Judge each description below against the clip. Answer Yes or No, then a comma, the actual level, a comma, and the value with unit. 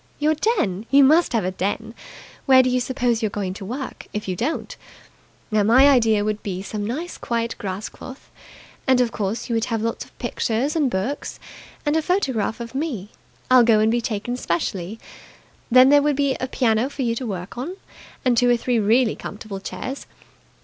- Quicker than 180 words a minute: Yes, average, 200 wpm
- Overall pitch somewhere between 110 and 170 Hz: No, high, 235 Hz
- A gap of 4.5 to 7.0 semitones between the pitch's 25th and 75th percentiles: No, average, 3.8 semitones